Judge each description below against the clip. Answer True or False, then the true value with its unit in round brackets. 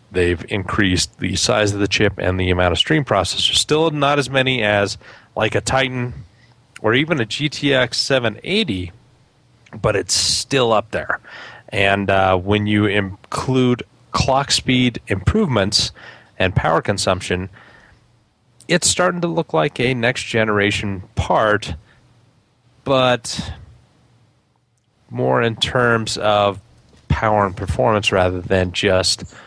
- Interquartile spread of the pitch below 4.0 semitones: False (4.5 semitones)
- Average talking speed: False (125 wpm)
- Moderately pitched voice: False (110 Hz)